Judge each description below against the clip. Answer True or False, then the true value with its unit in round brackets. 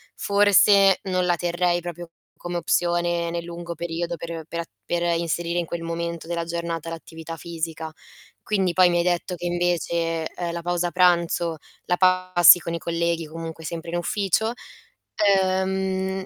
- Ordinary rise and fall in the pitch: False (1.2 semitones)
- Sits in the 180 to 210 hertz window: False (170 Hz)